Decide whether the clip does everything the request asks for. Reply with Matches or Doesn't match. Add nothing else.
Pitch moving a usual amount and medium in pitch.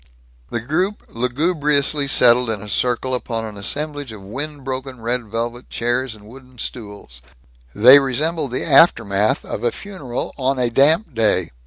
Doesn't match